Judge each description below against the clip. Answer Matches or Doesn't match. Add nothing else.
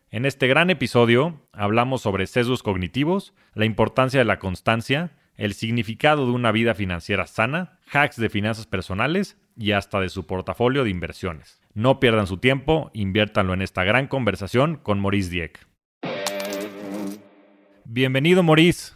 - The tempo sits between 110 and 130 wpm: Doesn't match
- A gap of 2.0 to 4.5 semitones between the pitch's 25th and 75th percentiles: Doesn't match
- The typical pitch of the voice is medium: Doesn't match